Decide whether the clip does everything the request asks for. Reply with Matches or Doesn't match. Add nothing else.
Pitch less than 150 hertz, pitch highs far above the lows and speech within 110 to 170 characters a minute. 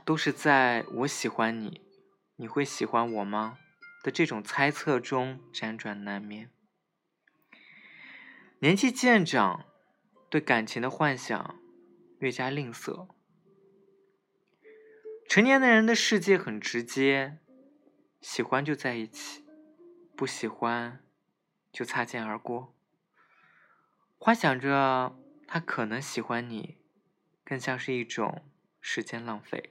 Matches